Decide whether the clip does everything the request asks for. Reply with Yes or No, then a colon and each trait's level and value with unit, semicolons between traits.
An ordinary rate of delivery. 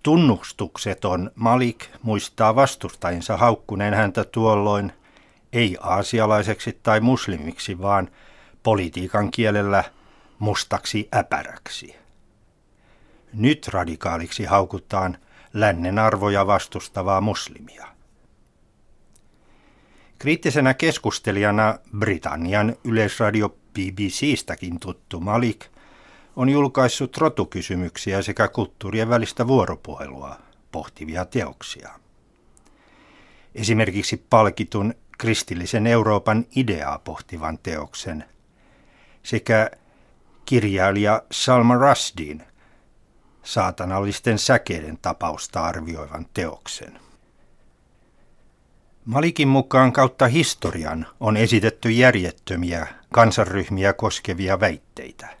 No: slow, 70 wpm